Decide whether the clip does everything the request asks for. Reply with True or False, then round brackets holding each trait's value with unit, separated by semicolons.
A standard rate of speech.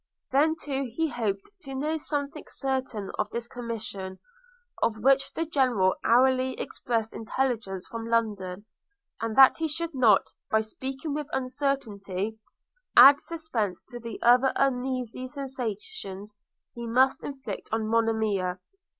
False (130 wpm)